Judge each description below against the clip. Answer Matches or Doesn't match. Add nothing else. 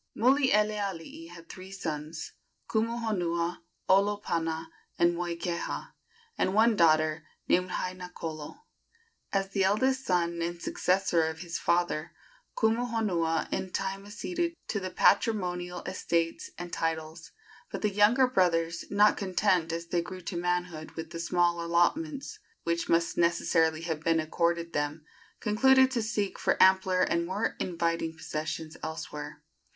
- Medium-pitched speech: Matches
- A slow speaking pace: Matches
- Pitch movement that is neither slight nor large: Matches